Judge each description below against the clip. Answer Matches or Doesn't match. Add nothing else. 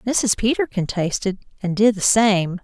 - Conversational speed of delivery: Matches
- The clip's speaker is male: Doesn't match